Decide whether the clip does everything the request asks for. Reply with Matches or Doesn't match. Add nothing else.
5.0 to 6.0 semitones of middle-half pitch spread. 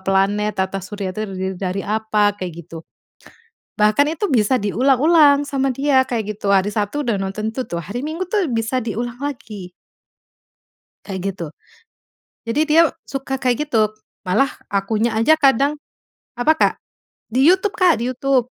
Matches